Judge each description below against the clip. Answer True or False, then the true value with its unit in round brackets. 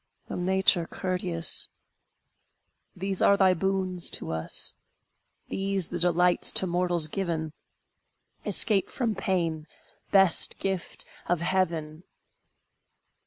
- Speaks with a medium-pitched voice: True (180 Hz)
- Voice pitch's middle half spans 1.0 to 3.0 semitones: True (2.4 semitones)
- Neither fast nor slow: False (100 wpm)